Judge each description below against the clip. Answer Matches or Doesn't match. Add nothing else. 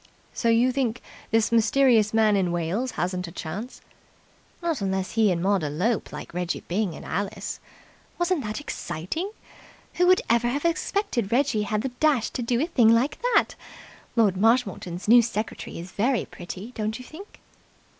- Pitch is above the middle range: Matches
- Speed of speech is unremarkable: Matches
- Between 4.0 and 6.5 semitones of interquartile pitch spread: Matches